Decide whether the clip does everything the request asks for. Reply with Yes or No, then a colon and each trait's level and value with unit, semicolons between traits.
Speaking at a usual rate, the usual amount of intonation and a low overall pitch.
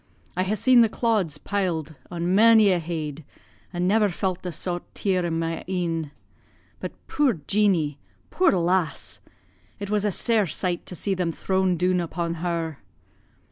No: average, 160 wpm; average, 3.3 semitones; medium, 180 Hz